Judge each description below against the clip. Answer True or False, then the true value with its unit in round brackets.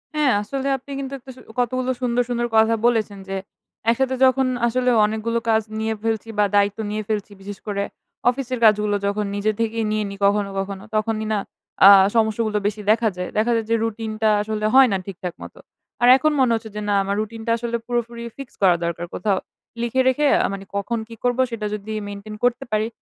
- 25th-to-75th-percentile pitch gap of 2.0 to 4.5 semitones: True (2.5 semitones)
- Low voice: False (220 Hz)